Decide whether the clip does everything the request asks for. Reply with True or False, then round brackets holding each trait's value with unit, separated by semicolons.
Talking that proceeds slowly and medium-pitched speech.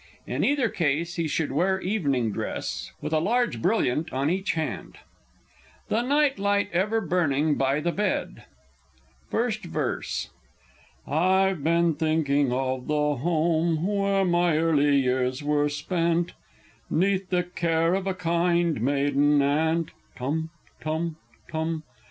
True (130 wpm; 165 Hz)